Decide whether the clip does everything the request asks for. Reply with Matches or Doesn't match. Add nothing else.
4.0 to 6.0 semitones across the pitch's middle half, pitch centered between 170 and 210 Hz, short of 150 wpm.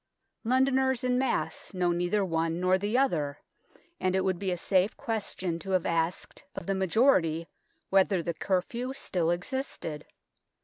Doesn't match